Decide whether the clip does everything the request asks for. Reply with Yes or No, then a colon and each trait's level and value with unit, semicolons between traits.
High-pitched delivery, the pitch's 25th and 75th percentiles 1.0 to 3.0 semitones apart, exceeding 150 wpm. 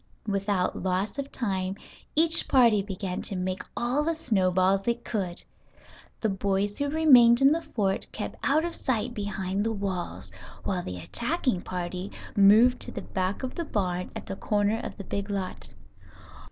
No: high, 205 Hz; average, 4.6 semitones; average, 165 wpm